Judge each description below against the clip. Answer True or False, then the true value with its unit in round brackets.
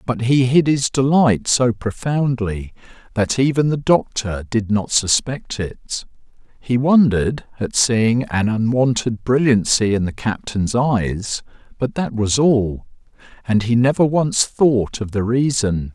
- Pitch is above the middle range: False (120 Hz)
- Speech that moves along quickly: False (145 wpm)